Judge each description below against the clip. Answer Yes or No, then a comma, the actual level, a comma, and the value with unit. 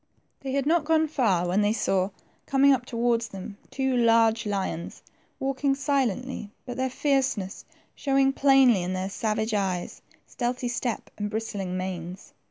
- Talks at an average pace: Yes, average, 150 wpm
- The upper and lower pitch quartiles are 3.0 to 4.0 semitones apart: No, wide, 5.5 semitones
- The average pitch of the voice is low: No, high, 235 Hz